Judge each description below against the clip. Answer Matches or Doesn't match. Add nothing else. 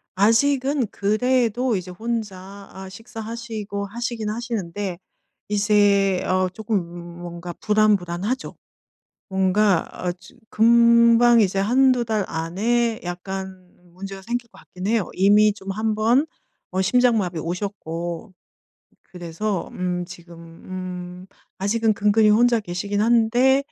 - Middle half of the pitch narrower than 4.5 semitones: Matches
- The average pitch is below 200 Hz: Doesn't match